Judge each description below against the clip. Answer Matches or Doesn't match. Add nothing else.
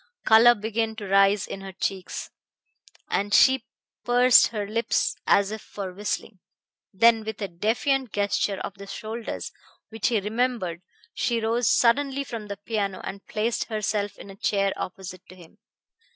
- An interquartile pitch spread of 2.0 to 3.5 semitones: Matches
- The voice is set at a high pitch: Matches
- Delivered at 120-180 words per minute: Matches